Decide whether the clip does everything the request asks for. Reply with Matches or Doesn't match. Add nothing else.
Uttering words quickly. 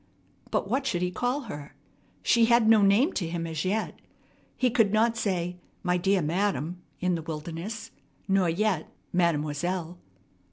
Doesn't match